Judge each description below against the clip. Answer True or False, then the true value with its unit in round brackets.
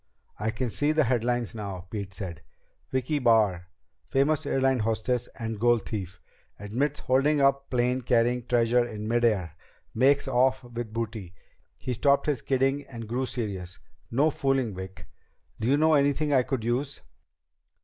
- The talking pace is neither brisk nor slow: True (155 wpm)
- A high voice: False (120 Hz)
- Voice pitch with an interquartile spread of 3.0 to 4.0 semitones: True (3.6 semitones)